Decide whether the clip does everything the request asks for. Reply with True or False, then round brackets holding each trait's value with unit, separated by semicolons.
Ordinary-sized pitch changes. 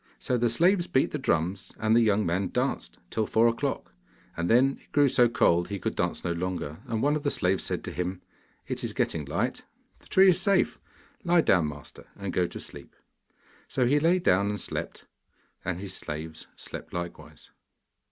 False (7.5 semitones)